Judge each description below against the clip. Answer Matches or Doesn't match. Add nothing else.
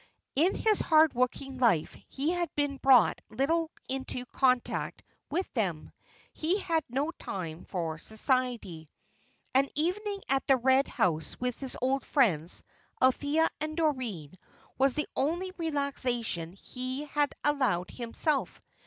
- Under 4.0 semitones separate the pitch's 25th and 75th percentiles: Doesn't match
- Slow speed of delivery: Matches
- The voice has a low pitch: Doesn't match